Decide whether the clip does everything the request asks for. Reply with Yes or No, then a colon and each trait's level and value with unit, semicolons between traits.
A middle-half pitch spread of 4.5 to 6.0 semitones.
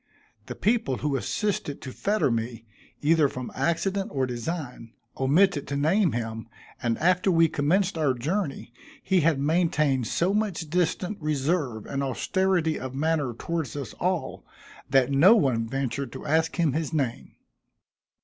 Yes: average, 5.0 semitones